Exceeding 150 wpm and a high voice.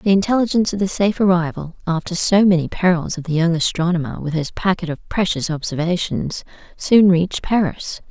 No: average, 170 wpm; medium, 175 Hz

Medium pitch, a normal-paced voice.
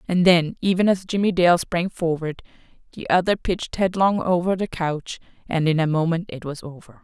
Yes: medium, 175 Hz; average, 190 wpm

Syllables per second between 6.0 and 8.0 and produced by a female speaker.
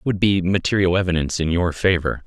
No: 6.3 syllables/s; male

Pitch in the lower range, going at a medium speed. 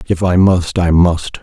No: very low, 90 Hz; fast, 210 wpm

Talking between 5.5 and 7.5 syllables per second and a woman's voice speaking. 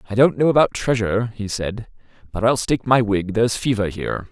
No: 5.9 syllables/s; male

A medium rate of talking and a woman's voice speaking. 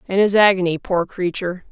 Yes: average, 175 wpm; female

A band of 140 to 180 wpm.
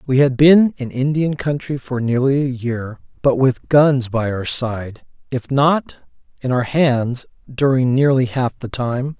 Yes: average, 170 wpm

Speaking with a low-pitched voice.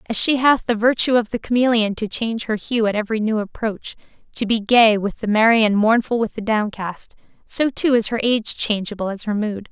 No: high, 220 Hz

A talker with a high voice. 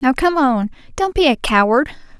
Yes: very high, 275 Hz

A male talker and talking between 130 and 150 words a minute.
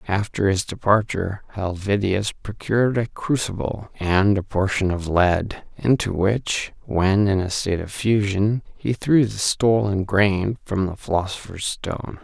Yes: male; average, 140 wpm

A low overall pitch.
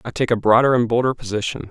Yes: low, 120 Hz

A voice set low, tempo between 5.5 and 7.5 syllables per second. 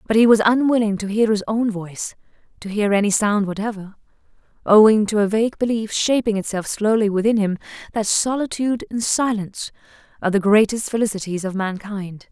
No: high, 210 Hz; 5.8 syllables/s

